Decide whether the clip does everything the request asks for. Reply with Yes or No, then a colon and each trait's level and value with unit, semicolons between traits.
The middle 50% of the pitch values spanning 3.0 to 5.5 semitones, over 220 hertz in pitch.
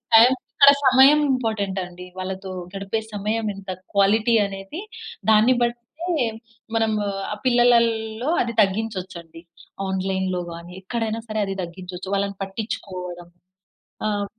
No: average, 3.3 semitones; high, 205 Hz